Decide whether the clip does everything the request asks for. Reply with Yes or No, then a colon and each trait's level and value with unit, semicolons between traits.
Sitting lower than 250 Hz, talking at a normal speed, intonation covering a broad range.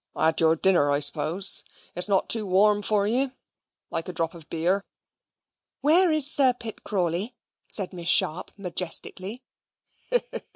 No: high, 190 Hz; average, 150 wpm; average, 4.6 semitones